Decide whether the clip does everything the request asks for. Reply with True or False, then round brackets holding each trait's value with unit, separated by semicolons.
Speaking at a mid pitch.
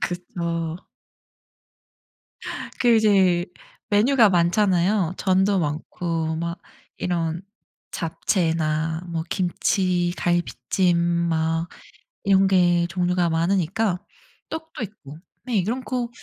True (175 Hz)